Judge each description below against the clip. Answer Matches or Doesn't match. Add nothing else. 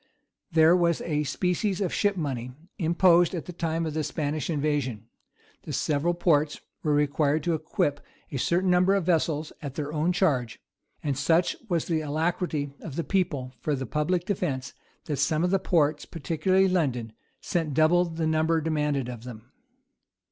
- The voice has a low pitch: Doesn't match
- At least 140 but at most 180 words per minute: Matches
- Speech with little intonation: Doesn't match